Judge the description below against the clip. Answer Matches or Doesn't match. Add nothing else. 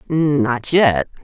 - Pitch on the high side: Doesn't match